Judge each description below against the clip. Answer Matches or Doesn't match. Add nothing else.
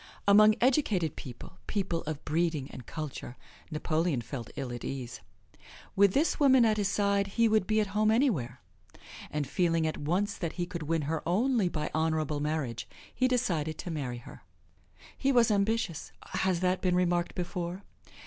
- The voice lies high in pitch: Doesn't match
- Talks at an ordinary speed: Matches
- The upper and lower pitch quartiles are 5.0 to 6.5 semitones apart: Matches